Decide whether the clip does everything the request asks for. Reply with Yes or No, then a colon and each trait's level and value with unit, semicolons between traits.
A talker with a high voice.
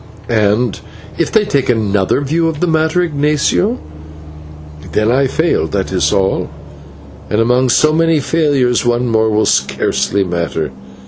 No: low, 125 Hz